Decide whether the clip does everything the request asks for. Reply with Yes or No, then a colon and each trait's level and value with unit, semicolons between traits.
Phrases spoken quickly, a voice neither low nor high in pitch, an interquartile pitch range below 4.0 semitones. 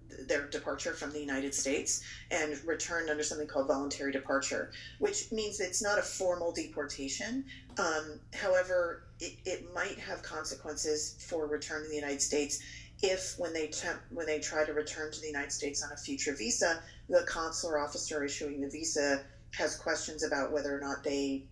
No: average, 175 wpm; medium, 150 Hz; narrow, 2.4 semitones